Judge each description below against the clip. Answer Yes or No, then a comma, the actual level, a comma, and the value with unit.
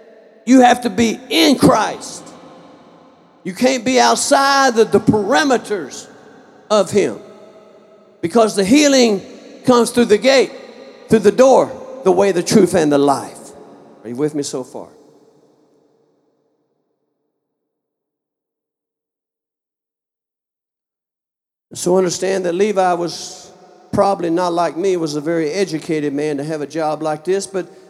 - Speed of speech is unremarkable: No, slow, 125 wpm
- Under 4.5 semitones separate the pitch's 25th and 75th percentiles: No, wide, 5.4 semitones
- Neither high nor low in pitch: No, high, 205 Hz